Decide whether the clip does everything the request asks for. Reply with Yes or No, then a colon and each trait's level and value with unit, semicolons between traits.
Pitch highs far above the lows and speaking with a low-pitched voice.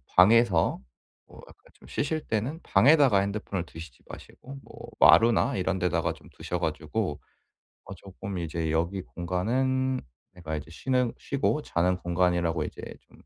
Yes: wide, 5.8 semitones; very low, 95 Hz